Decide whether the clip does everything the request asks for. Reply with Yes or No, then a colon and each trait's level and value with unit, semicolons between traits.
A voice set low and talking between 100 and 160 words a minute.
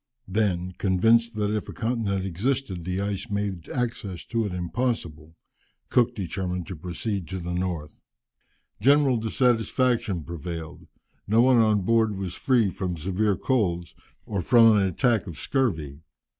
Yes: low, 100 Hz; average, 145 wpm